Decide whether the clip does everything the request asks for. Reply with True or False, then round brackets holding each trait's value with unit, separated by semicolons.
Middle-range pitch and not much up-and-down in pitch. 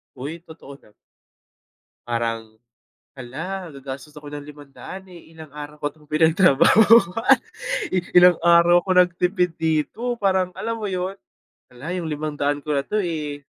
False (160 Hz; 3.9 semitones)